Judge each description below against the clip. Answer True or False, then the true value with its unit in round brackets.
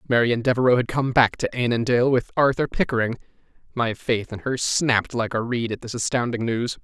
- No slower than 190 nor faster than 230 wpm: True (195 wpm)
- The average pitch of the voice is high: False (120 Hz)